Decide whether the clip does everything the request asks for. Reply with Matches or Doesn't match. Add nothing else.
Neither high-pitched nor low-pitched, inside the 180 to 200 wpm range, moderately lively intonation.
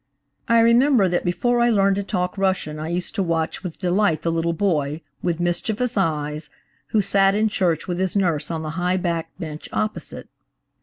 Matches